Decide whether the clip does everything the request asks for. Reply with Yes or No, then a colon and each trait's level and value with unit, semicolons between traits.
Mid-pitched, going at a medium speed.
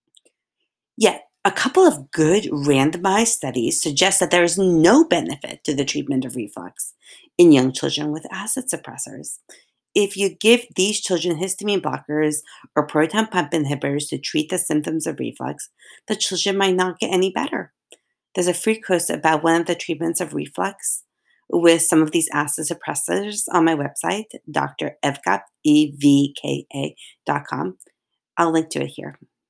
Yes: medium, 170 Hz; average, 155 wpm